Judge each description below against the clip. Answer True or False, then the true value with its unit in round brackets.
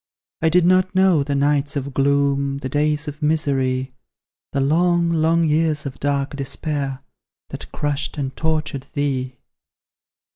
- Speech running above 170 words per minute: False (140 wpm)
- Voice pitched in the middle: True (145 Hz)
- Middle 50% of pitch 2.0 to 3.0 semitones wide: True (2.4 semitones)